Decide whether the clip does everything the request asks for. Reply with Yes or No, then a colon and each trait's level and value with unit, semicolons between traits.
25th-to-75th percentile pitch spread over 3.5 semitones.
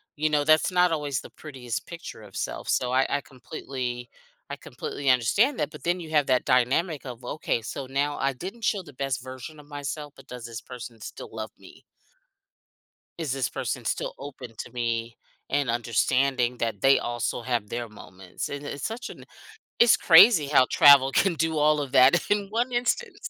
Yes: average, 4.1 semitones